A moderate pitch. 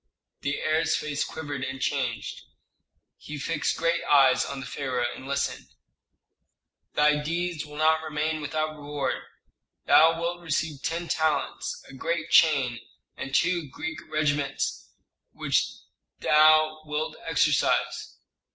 Yes: medium, 150 Hz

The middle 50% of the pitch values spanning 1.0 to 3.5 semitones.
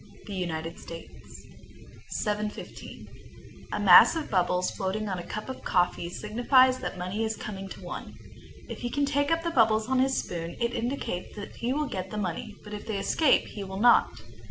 No: average, 5.3 semitones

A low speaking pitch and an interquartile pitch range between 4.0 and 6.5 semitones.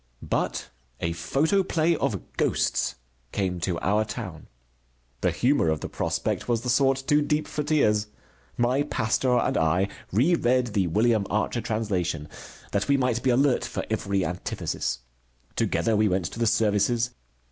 Yes: low, 115 Hz; average, 5.2 semitones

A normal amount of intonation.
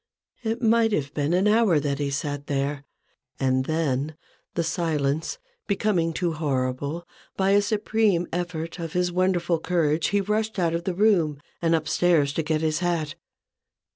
Yes: average, 3.8 semitones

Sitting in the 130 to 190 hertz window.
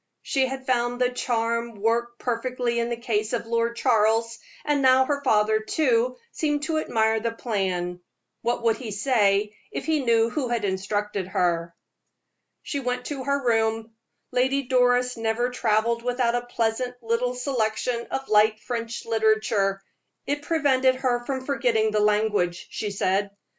No: high, 235 Hz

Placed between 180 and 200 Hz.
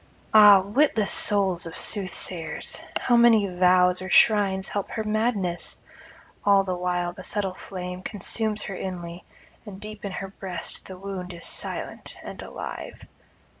Yes: high, 190 Hz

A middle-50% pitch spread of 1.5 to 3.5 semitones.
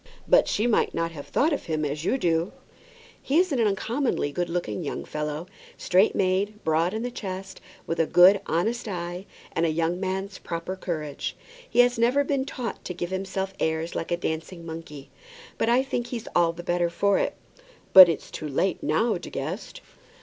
No: average, 4.6 semitones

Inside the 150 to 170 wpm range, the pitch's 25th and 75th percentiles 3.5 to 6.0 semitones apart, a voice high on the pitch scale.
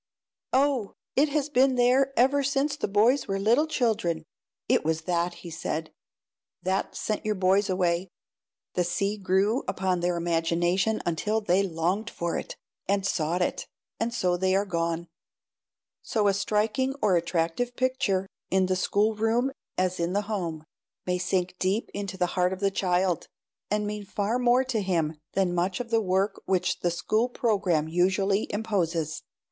Yes: average, 165 wpm; average, 3.9 semitones; high, 195 Hz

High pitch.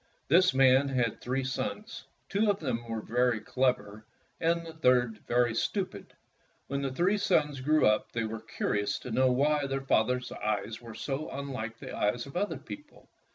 No: low, 130 Hz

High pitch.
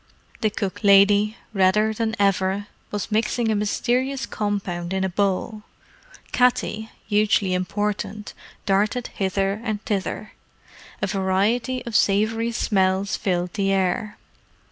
Yes: high, 205 Hz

